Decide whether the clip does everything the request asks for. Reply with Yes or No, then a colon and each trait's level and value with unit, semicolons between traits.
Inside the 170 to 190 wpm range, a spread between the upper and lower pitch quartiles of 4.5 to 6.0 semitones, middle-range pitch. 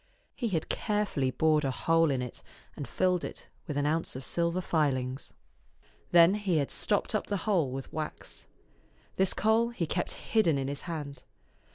Yes: average, 175 wpm; average, 5.1 semitones; medium, 165 Hz